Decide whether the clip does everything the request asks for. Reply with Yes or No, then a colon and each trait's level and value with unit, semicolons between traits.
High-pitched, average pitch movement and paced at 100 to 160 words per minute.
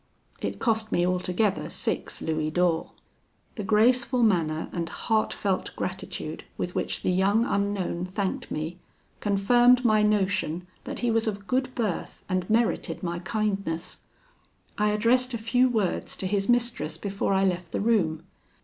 Yes: high, 200 Hz; average, 4.0 semitones; average, 150 wpm